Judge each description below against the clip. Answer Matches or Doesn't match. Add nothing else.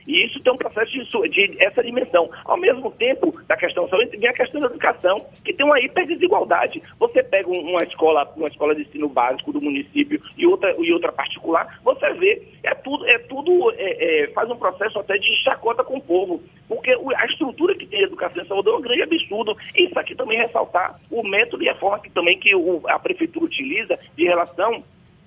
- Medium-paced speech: Doesn't match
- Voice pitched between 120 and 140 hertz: Doesn't match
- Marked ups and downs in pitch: Matches